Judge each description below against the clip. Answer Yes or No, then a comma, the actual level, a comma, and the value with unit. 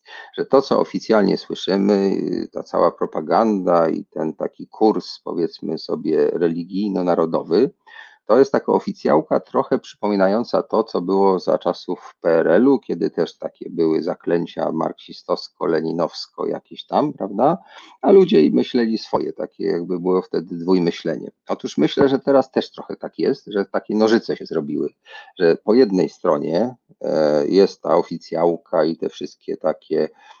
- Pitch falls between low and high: No, low, 105 Hz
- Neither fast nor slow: Yes, average, 135 wpm